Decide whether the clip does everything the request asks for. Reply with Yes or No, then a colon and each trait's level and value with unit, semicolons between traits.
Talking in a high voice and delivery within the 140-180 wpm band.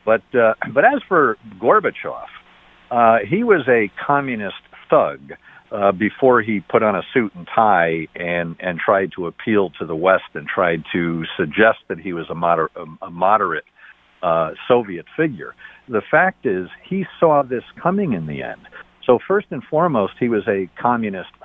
No: very low, 95 Hz; average, 170 wpm